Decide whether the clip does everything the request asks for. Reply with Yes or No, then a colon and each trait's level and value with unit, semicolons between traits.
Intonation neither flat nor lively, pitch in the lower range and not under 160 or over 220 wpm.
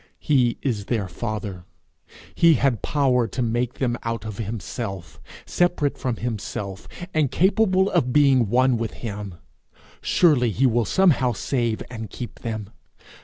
No: average, 3.8 semitones; low, 120 Hz; average, 140 wpm